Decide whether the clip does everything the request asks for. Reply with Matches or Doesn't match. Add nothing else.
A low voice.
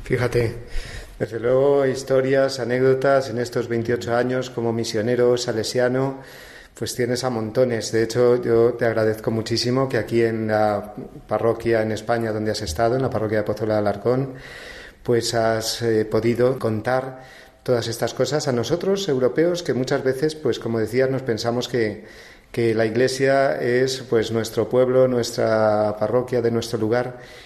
Matches